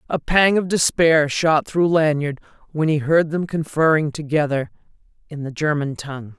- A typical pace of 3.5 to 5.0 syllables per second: Yes, 4.7 syllables/s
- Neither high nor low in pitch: Yes, medium, 155 Hz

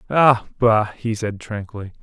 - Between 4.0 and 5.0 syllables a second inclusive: Yes, 4.6 syllables/s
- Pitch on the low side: Yes, low, 110 Hz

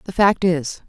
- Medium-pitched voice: Yes, medium, 175 Hz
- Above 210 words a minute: No, fast, 205 wpm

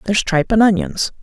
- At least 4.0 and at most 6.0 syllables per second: No, 6.9 syllables/s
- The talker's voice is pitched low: No, high, 200 Hz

